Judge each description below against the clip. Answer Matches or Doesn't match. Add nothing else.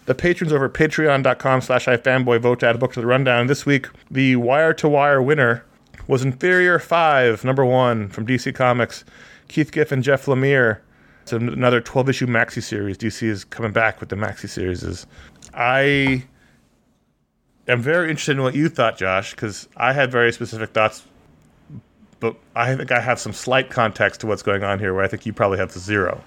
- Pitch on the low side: Matches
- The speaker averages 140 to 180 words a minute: Doesn't match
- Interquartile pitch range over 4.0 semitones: Doesn't match